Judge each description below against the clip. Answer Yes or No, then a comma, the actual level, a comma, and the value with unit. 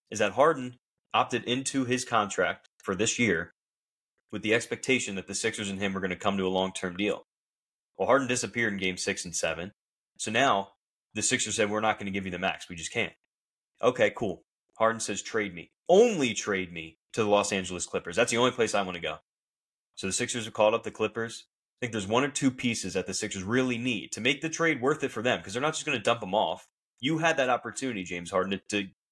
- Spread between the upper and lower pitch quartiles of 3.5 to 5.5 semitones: Yes, average, 4.4 semitones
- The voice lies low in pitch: Yes, low, 110 Hz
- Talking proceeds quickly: Yes, fast, 245 wpm